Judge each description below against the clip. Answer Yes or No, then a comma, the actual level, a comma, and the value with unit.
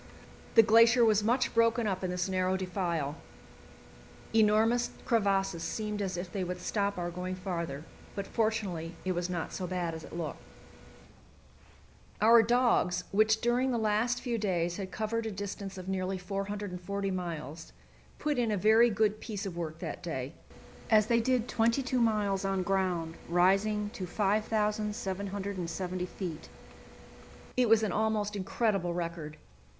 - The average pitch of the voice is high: Yes, high, 200 Hz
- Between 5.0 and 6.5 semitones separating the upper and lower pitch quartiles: No, average, 3.3 semitones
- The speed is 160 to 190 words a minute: No, average, 150 wpm